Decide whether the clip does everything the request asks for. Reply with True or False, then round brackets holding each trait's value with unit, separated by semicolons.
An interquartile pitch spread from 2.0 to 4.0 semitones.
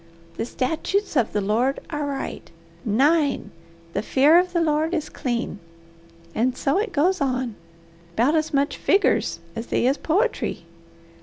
False (4.6 semitones)